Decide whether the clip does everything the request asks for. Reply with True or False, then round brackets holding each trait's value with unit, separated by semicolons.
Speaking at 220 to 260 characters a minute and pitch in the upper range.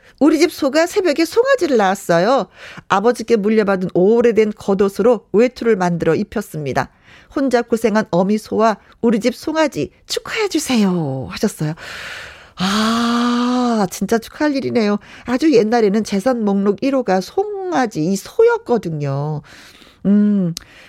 False (285 characters per minute; 225 Hz)